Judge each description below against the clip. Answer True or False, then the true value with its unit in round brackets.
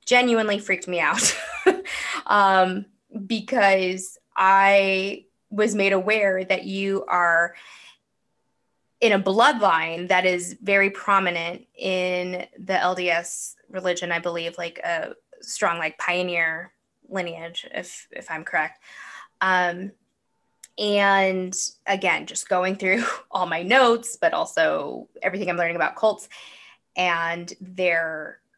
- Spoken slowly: True (115 wpm)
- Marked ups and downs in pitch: False (2.4 semitones)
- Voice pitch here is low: False (190 Hz)